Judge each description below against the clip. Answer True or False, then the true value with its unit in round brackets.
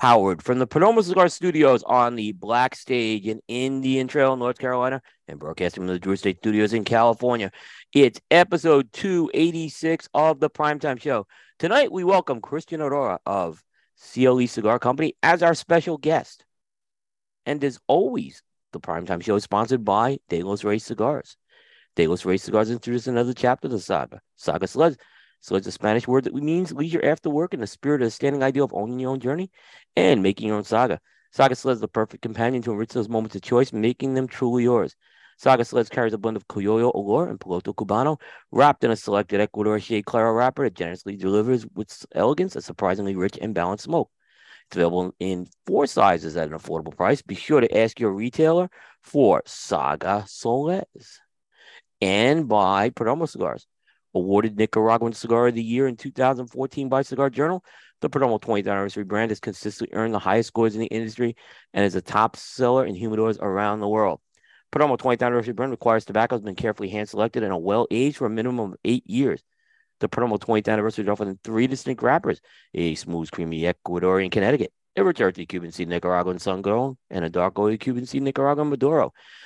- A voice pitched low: True (115 Hz)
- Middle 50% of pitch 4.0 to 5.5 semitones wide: True (4.4 semitones)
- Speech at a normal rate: True (185 wpm)